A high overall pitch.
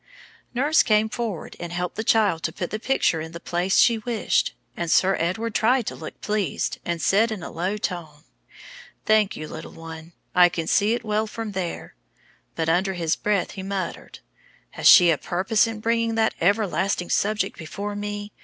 Yes: high, 200 Hz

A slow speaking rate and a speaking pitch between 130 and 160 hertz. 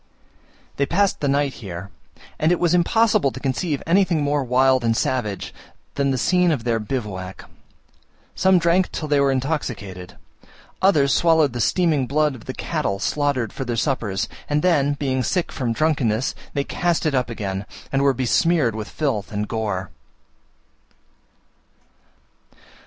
No: average, 150 wpm; low, 135 Hz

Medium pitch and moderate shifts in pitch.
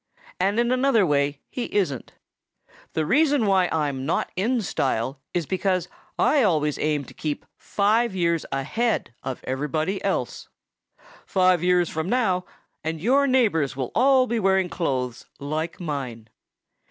No: medium, 180 Hz; wide, 6.8 semitones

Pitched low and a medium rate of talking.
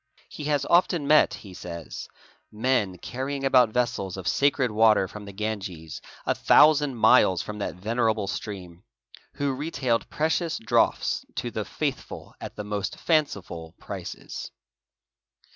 Yes: low, 110 Hz; average, 145 wpm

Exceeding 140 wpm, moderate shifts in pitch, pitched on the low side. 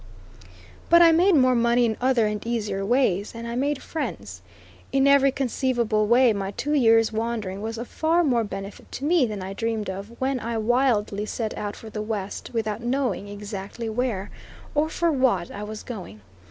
No: average, 185 wpm; average, 3.9 semitones; high, 230 Hz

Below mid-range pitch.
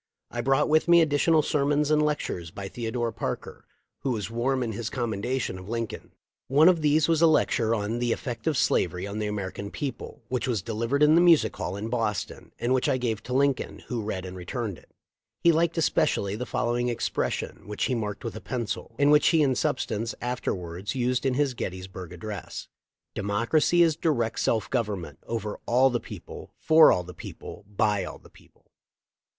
Yes: low, 120 Hz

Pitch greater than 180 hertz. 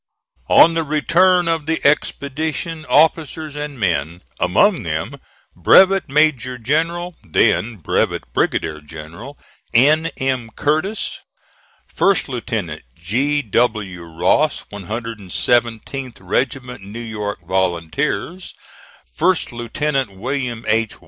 No: low, 125 Hz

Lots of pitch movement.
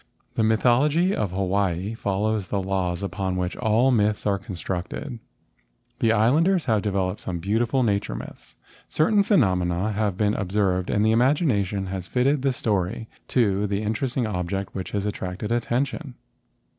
No: average, 3.9 semitones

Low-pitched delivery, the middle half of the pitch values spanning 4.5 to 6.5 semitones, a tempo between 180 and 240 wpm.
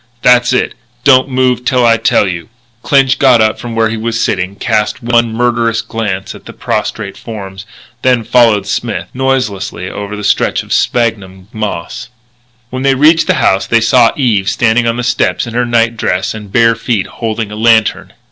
No: low, 115 Hz; average, 2.8 semitones; average, 185 wpm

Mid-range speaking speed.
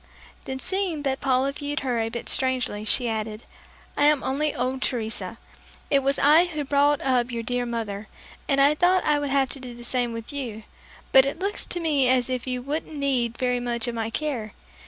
No: fast, 210 wpm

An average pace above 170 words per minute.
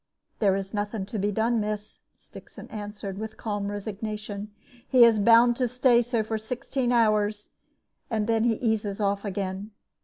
No: average, 160 wpm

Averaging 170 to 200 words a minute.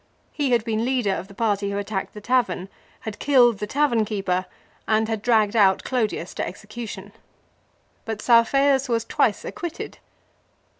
No: average, 155 wpm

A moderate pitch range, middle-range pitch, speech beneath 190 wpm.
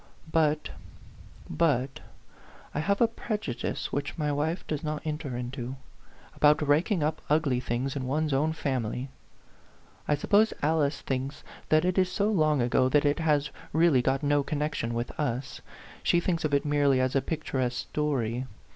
Yes: average, 3.0 semitones; medium, 145 Hz; average, 165 wpm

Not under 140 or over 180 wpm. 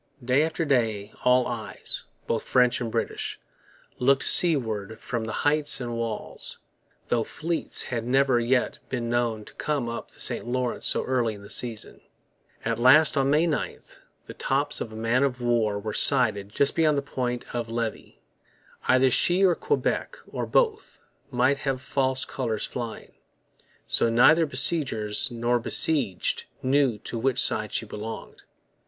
Yes: average, 160 wpm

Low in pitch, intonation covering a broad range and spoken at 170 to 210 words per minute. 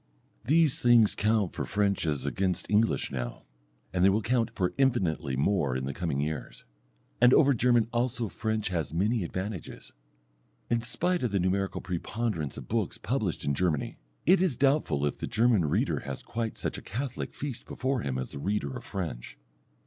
Yes: low, 100 Hz; wide, 6.9 semitones; average, 180 wpm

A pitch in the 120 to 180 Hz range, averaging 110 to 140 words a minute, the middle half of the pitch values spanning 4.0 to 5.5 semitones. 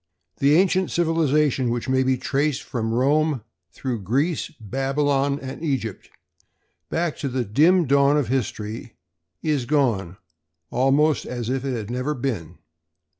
No: low, 135 Hz; slow, 135 wpm; average, 3.6 semitones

